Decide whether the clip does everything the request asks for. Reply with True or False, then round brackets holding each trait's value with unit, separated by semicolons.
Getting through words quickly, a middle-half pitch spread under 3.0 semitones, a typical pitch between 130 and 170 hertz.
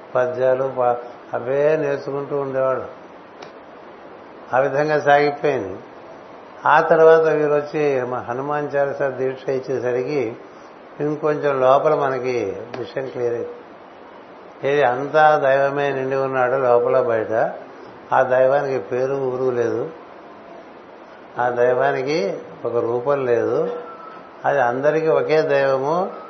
False (100 wpm; 2.4 semitones; 135 Hz)